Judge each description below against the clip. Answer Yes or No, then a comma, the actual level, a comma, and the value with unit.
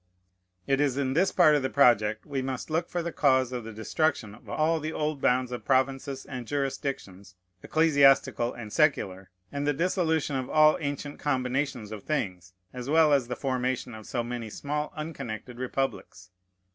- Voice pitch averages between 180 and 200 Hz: No, low, 135 Hz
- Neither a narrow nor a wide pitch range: Yes, average, 3.6 semitones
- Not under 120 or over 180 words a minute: Yes, average, 175 wpm